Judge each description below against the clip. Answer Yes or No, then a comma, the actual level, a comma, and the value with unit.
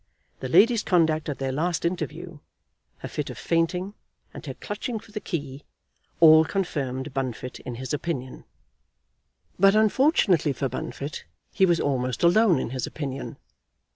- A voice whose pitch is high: No, medium, 160 Hz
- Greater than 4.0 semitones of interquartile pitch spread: Yes, wide, 5.4 semitones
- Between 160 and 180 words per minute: No, average, 145 wpm